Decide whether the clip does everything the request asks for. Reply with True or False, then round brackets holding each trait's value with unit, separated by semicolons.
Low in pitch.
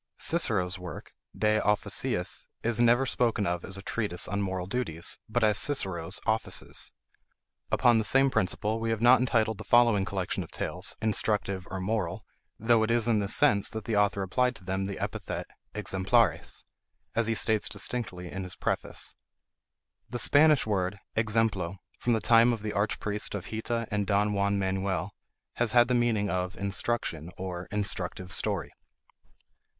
True (105 Hz)